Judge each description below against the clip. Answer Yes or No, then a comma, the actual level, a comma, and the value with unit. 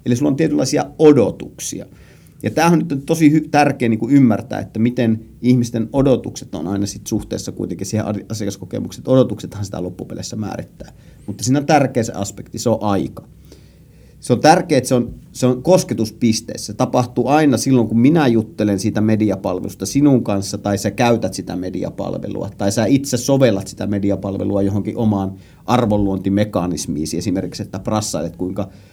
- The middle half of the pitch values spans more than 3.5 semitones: Yes, average, 4.1 semitones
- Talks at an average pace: No, fast, 160 wpm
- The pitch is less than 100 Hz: No, low, 110 Hz